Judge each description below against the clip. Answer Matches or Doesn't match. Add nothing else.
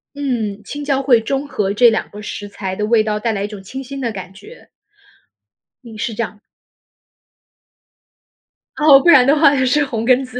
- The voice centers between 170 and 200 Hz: Doesn't match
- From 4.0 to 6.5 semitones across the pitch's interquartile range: Matches